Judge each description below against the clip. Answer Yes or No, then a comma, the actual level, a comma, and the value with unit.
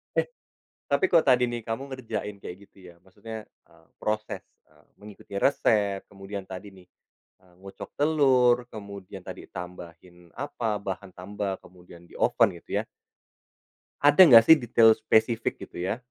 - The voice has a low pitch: Yes, low, 105 Hz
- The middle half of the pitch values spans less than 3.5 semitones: No, average, 4.3 semitones